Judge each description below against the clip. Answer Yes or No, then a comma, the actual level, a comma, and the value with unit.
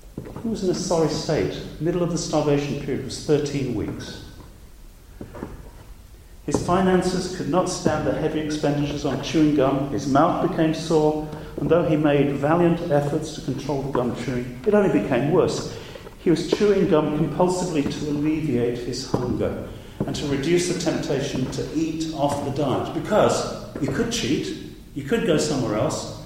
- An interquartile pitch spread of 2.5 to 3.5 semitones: Yes, average, 2.8 semitones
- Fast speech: No, average, 165 wpm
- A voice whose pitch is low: No, medium, 150 Hz